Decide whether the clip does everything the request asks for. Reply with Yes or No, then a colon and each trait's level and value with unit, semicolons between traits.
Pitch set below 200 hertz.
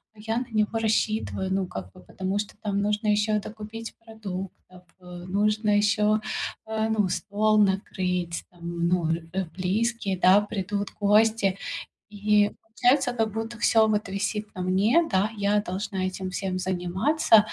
No: high, 205 Hz